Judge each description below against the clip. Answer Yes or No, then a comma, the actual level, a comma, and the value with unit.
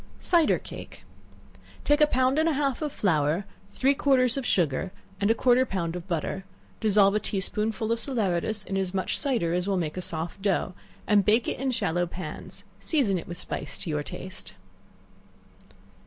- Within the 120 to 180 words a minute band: No, average, 195 wpm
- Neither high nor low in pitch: No, high, 200 Hz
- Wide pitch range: Yes, wide, 6.2 semitones